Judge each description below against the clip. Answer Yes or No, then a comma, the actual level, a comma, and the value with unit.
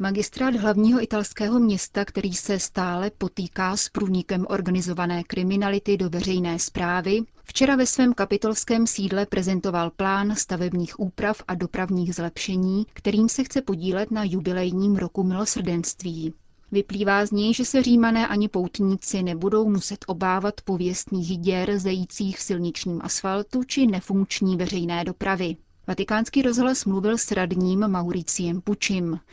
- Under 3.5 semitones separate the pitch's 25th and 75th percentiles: Yes, narrow, 2.5 semitones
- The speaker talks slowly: No, average, 130 wpm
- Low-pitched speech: No, high, 195 Hz